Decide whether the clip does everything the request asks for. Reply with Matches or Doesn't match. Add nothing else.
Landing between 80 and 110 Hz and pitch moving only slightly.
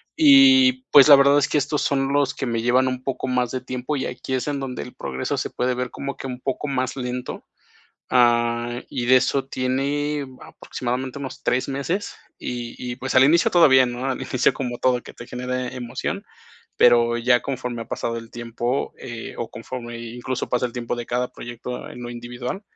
Doesn't match